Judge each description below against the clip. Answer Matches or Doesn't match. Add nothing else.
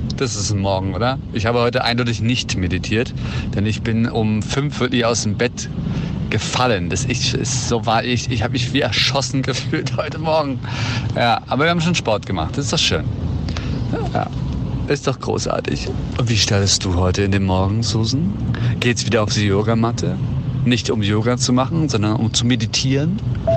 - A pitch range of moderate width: Matches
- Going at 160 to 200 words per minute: Matches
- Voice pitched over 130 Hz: Doesn't match